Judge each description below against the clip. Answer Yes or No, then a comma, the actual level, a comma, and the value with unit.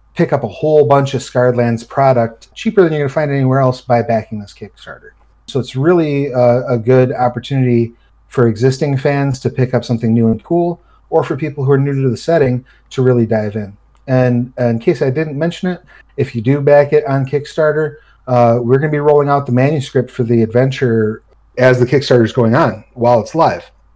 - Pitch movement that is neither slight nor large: Yes, average, 3.3 semitones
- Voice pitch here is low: Yes, low, 130 Hz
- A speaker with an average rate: No, fast, 215 wpm